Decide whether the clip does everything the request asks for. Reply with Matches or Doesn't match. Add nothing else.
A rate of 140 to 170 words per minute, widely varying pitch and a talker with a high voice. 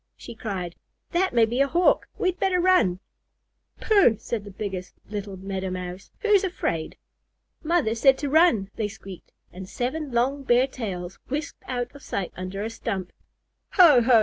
Matches